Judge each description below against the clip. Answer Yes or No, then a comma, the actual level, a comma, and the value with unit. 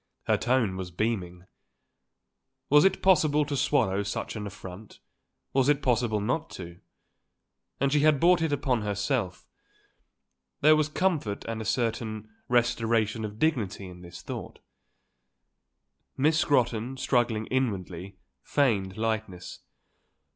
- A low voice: Yes, low, 115 Hz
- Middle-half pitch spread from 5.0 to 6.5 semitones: Yes, wide, 5.6 semitones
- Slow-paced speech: Yes, slow, 125 wpm